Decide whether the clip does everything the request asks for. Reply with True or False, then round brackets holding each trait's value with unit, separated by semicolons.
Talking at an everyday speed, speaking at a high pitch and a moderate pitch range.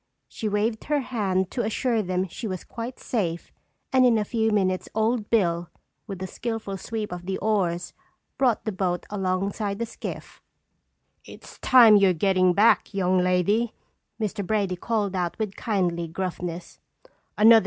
True (155 wpm; 200 Hz; 3.3 semitones)